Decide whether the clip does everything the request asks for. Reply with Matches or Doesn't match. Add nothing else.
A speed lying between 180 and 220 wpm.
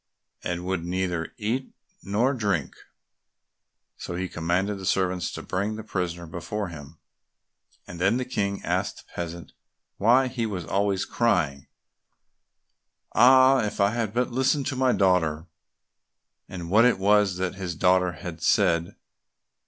Doesn't match